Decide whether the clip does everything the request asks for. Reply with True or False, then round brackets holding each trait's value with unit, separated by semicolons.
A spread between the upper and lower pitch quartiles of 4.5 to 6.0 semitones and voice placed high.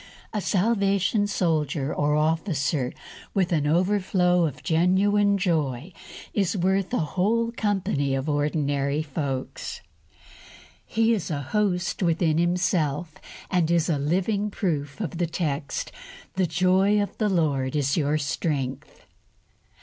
False (4.8 semitones; 170 Hz)